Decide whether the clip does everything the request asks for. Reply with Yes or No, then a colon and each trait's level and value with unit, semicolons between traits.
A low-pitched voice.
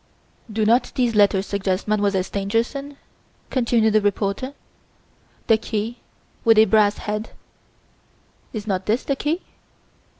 No: high, 215 Hz